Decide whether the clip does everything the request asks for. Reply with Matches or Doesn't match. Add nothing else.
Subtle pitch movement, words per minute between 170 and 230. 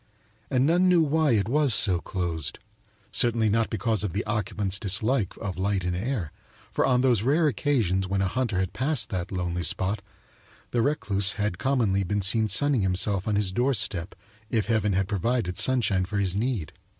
Doesn't match